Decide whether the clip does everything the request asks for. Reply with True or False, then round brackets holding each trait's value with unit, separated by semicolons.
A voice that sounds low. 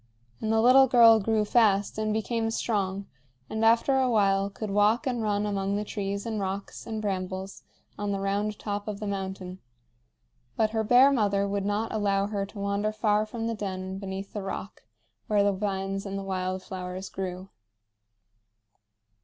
False (205 Hz)